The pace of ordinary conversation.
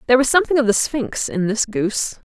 No: fast, 235 wpm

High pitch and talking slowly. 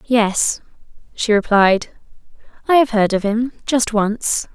Yes: high, 225 Hz; slow, 120 wpm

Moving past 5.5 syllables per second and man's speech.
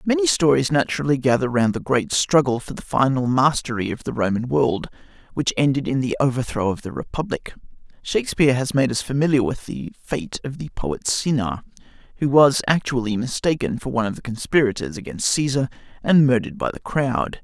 Yes: 5.7 syllables/s; male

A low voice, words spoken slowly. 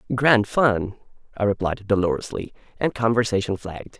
Yes: low, 105 Hz; slow, 120 wpm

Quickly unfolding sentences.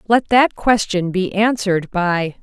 No: average, 150 wpm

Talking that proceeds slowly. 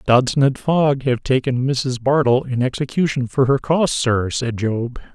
No: average, 175 wpm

